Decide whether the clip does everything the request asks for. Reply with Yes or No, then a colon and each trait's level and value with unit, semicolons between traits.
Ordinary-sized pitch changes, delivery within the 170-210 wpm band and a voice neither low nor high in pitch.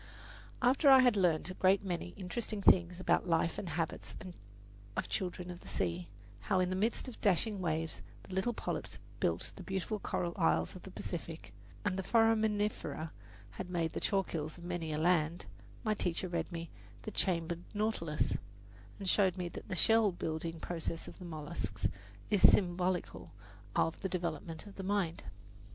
Yes: average, 3.2 semitones; average, 175 wpm; medium, 180 Hz